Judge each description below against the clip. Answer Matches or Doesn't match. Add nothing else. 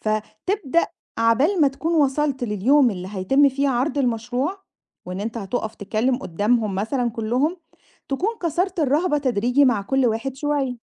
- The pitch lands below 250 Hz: Doesn't match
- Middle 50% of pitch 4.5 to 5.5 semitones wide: Matches